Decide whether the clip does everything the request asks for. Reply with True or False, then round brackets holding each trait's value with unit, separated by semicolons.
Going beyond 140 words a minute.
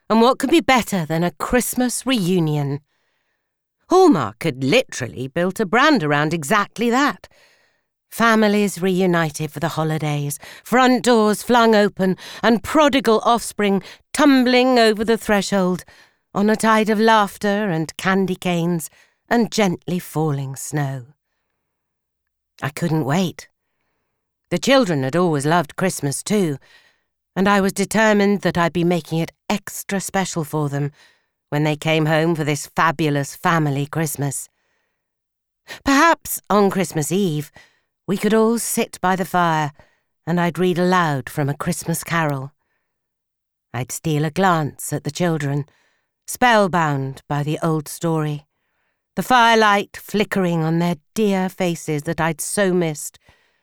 False (135 wpm)